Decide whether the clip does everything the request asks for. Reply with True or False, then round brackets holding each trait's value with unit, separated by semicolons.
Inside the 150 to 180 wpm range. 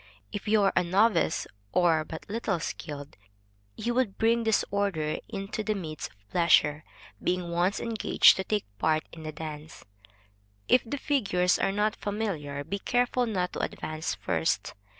True (155 wpm)